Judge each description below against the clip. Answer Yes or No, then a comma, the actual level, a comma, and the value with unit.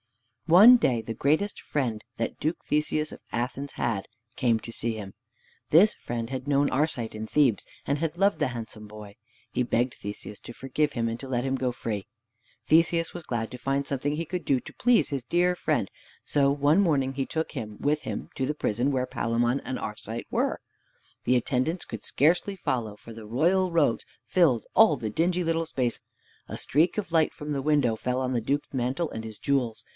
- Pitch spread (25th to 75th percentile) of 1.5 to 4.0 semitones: No, average, 5.0 semitones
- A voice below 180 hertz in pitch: Yes, low, 135 Hz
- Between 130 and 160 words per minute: No, average, 200 wpm